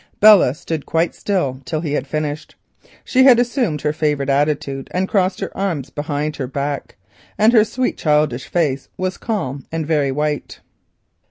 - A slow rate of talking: No, average, 165 wpm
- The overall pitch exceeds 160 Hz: No, medium, 155 Hz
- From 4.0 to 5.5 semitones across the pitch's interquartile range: Yes, average, 4.6 semitones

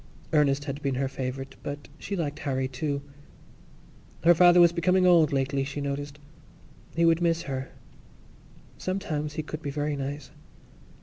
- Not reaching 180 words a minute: Yes, average, 150 wpm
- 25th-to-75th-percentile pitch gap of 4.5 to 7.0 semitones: No, average, 3.2 semitones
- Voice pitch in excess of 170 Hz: No, medium, 145 Hz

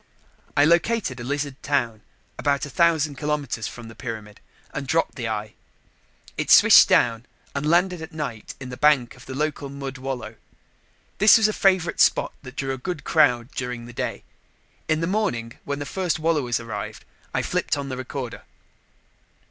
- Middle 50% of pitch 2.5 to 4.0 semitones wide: No, average, 4.4 semitones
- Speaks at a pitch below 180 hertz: Yes, medium, 140 Hz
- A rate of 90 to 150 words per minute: No, average, 175 wpm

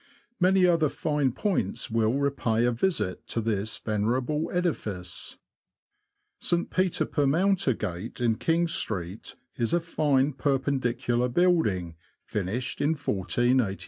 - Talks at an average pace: No, slow, 115 wpm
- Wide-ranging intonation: Yes, wide, 6.7 semitones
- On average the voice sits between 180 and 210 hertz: No, low, 130 Hz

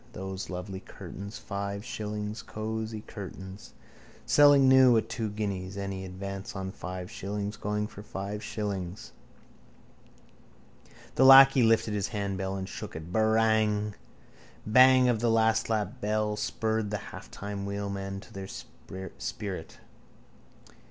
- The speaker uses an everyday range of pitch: No, narrow, 2.1 semitones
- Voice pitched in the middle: No, low, 105 Hz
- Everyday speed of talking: No, slow, 120 wpm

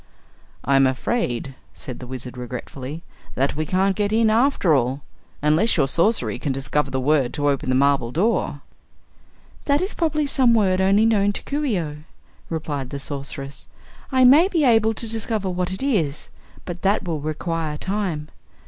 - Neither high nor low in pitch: Yes, medium, 165 Hz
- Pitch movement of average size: No, wide, 8.0 semitones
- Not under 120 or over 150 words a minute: No, average, 170 wpm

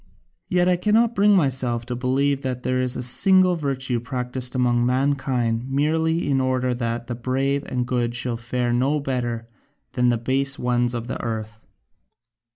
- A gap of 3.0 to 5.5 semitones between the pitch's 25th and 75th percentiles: No, narrow, 2.5 semitones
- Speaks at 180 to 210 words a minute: No, average, 165 wpm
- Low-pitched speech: Yes, low, 130 Hz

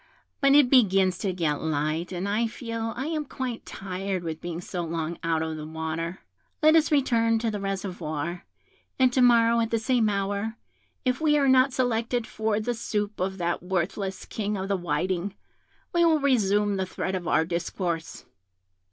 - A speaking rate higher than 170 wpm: Yes, average, 180 wpm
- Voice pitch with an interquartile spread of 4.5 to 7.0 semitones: Yes, average, 5.2 semitones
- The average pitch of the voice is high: Yes, high, 200 Hz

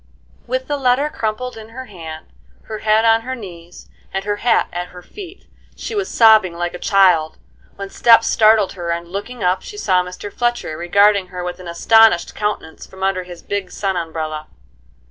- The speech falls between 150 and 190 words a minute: Yes, average, 185 wpm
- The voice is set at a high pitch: Yes, high, 195 Hz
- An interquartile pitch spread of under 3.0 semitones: No, average, 4.2 semitones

